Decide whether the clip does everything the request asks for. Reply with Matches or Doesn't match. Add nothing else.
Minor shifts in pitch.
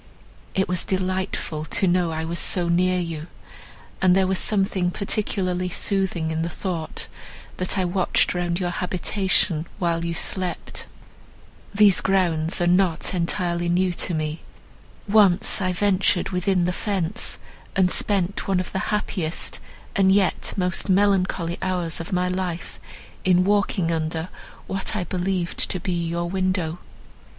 Matches